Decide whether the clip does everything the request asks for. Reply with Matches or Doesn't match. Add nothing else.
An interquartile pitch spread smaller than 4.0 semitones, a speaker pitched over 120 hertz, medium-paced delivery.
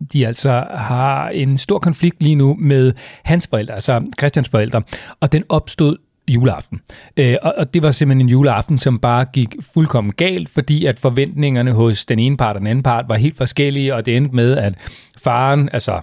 Matches